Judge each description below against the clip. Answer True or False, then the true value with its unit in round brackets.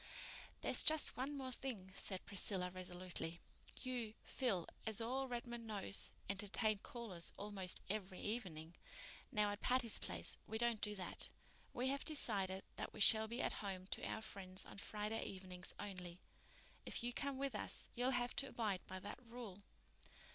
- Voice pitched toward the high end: True (210 Hz)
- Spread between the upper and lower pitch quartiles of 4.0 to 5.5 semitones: True (4.3 semitones)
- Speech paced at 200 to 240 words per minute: False (160 wpm)